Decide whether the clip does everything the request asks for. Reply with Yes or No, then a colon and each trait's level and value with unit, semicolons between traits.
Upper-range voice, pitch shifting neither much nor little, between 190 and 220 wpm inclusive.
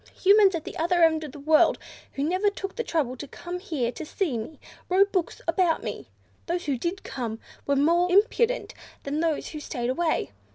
Yes: very high, 325 Hz; average, 4.5 semitones; average, 200 wpm